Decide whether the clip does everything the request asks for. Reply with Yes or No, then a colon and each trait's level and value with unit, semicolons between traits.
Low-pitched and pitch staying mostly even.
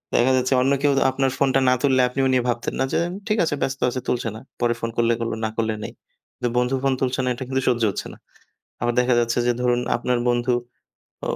Yes: low, 125 Hz; narrow, 1.7 semitones